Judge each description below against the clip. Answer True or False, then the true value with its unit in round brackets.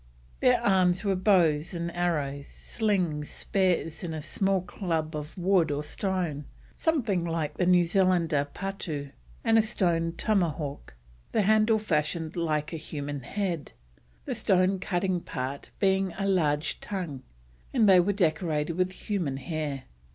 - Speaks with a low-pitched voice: False (175 Hz)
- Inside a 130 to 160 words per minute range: True (145 wpm)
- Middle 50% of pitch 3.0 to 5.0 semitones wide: True (4.1 semitones)